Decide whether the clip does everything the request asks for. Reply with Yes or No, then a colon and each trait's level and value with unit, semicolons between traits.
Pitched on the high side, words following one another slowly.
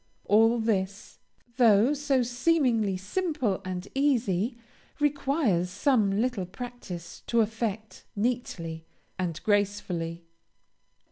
Yes: high, 220 Hz; slow, 90 wpm